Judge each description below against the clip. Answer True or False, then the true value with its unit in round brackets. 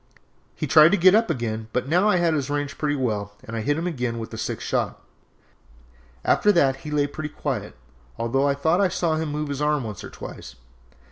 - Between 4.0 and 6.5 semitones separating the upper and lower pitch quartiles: True (4.4 semitones)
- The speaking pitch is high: False (145 Hz)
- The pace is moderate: False (215 wpm)